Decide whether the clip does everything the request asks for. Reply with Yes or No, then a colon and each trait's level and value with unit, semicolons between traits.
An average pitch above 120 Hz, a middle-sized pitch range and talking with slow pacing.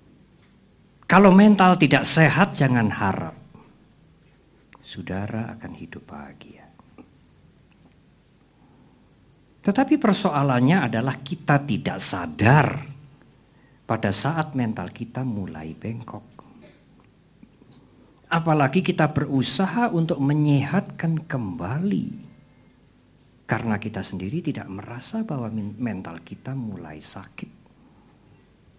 No: low, 135 Hz; wide, 6.7 semitones; slow, 80 wpm